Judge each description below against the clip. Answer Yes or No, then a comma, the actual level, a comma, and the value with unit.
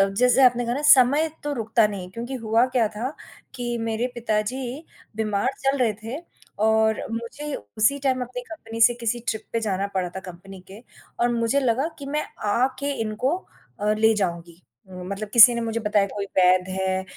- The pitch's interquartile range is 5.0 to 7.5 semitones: No, average, 3.3 semitones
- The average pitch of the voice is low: No, high, 225 Hz